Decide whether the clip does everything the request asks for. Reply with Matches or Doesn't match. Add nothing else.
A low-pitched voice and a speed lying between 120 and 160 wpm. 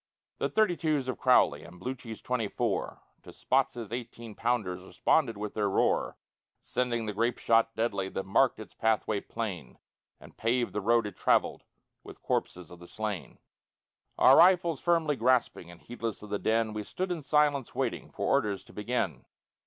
Doesn't match